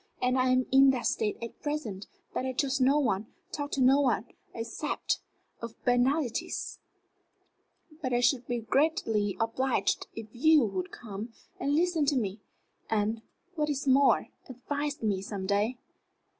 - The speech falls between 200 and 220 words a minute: No, average, 155 wpm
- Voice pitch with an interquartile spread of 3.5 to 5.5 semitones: Yes, average, 4.2 semitones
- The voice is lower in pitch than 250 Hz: No, very high, 255 Hz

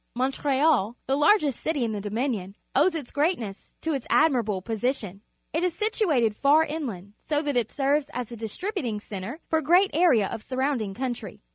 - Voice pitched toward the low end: No, very high, 265 Hz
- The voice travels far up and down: Yes, wide, 5.9 semitones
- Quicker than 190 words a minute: Yes, average, 200 wpm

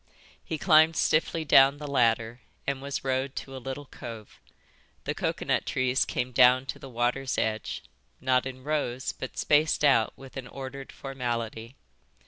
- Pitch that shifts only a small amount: Yes, narrow, 2.2 semitones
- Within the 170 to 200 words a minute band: No, average, 155 wpm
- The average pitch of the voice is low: Yes, low, 130 Hz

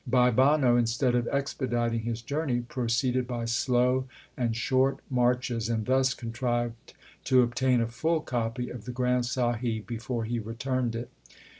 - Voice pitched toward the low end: Yes, low, 120 Hz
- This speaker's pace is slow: No, average, 150 wpm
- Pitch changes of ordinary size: No, narrow, 1.6 semitones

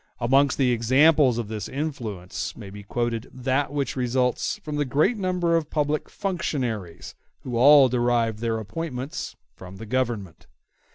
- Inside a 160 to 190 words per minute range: No, average, 150 wpm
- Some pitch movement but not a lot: Yes, average, 4.4 semitones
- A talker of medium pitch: No, low, 125 Hz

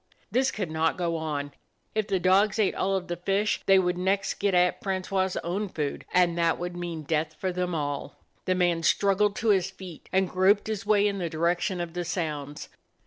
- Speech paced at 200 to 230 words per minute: Yes, fast, 205 wpm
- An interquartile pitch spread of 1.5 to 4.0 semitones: Yes, narrow, 2.6 semitones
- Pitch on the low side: No, medium, 180 Hz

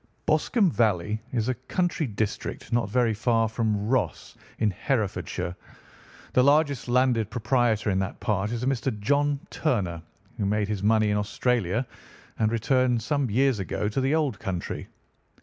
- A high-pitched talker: No, low, 115 Hz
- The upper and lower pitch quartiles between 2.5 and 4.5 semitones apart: Yes, average, 3.8 semitones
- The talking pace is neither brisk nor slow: Yes, average, 155 wpm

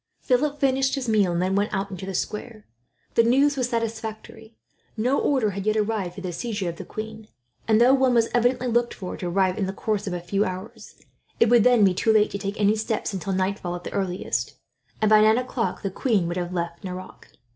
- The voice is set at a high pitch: Yes, high, 215 Hz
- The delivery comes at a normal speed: No, fast, 230 wpm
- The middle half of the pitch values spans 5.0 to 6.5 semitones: No, average, 3.7 semitones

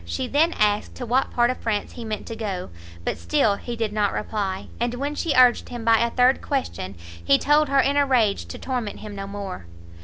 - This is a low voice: No, high, 230 Hz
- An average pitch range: Yes, average, 3.9 semitones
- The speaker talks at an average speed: No, fast, 225 wpm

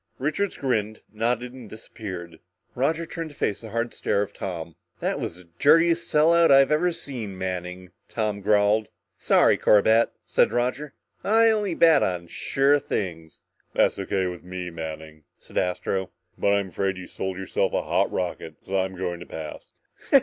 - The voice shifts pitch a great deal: Yes, wide, 7.1 semitones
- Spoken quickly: No, average, 165 wpm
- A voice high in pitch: No, low, 105 Hz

